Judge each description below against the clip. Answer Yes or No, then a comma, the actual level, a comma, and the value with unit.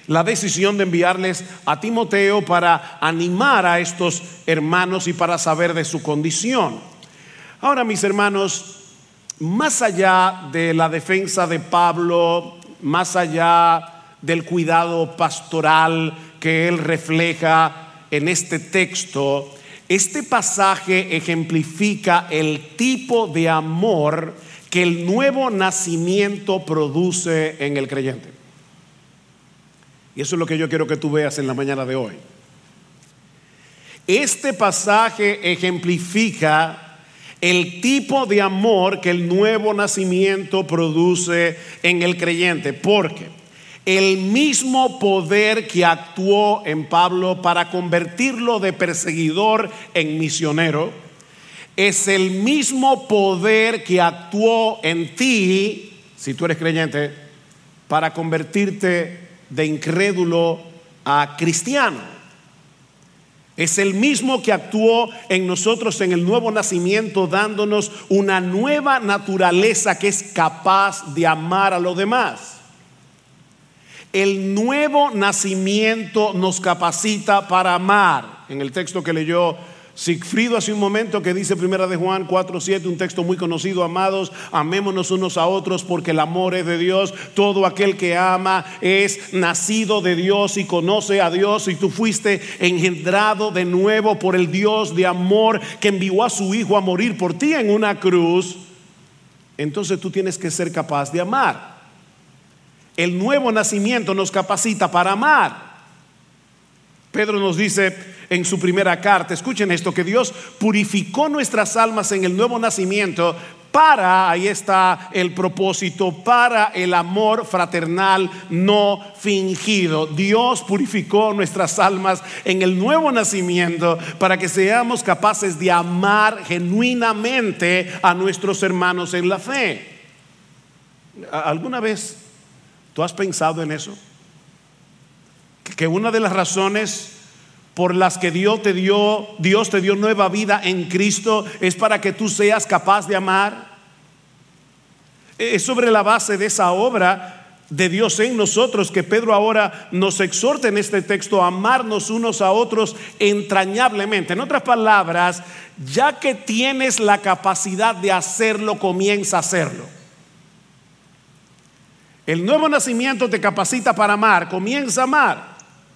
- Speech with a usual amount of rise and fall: Yes, average, 3.3 semitones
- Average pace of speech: No, slow, 130 wpm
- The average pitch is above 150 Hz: Yes, medium, 185 Hz